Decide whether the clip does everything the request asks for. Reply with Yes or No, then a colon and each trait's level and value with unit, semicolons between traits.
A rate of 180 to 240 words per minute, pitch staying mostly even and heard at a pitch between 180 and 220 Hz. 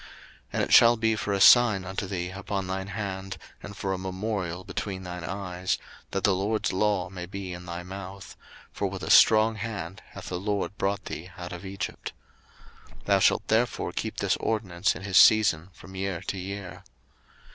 No: average, 190 wpm; narrow, 1.9 semitones; very low, 95 Hz